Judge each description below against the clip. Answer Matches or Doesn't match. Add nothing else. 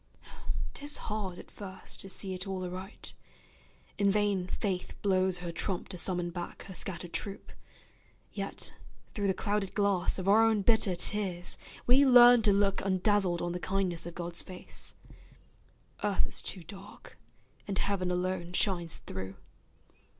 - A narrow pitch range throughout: Matches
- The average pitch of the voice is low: Doesn't match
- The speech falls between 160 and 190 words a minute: Doesn't match